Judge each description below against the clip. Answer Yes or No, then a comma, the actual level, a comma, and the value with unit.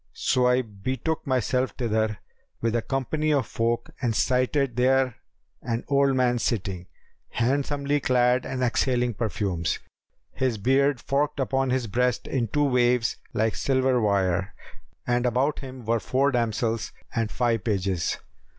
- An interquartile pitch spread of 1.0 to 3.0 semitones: Yes, average, 2.7 semitones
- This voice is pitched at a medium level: No, low, 125 Hz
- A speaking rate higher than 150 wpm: No, average, 140 wpm